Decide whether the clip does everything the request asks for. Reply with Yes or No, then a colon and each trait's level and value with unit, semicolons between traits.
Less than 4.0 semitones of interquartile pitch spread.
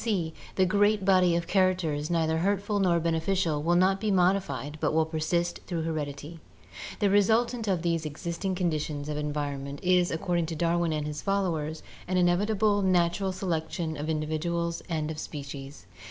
Yes: average, 3.3 semitones